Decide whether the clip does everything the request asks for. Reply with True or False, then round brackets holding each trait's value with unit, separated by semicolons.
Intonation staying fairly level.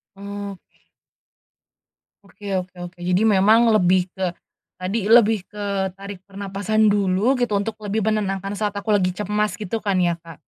True (2.0 semitones)